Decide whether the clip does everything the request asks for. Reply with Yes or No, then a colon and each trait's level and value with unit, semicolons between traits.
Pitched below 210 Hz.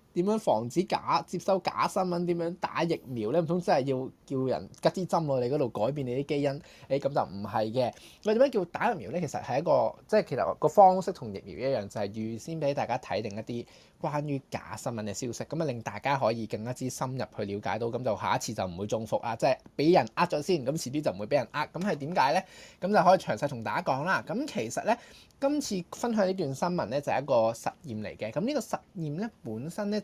Yes: medium, 140 Hz